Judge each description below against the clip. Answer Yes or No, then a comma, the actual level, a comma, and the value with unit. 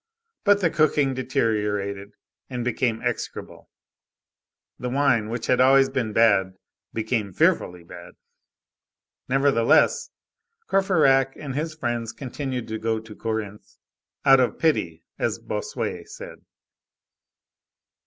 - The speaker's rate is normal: No, slow, 105 wpm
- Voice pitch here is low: Yes, low, 120 Hz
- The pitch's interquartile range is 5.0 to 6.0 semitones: No, average, 3.8 semitones